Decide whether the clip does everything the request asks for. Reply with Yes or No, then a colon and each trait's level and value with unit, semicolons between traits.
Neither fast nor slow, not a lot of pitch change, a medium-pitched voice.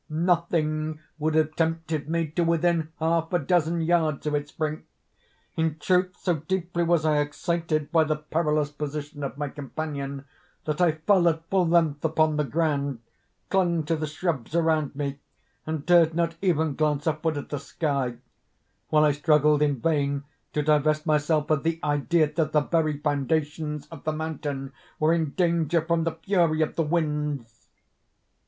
Yes: average, 165 wpm; narrow, 1.9 semitones; medium, 155 Hz